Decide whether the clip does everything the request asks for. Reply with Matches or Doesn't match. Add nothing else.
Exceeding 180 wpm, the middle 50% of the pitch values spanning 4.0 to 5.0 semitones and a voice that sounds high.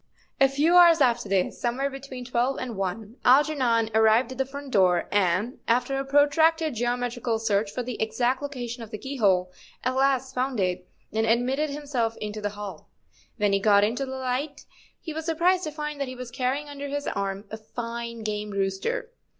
Matches